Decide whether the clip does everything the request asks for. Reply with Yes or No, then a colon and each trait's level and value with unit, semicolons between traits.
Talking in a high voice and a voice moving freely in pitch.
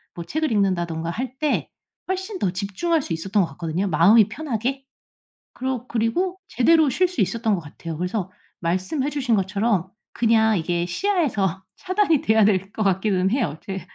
Yes: high, 215 Hz; wide, 6.7 semitones